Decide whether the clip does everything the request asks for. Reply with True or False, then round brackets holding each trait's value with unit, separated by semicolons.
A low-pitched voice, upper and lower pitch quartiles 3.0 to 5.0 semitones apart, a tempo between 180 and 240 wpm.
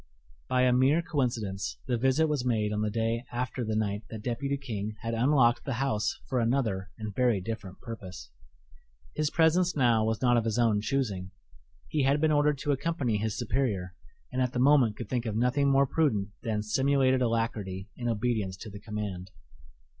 True (120 Hz; 4.0 semitones; 185 wpm)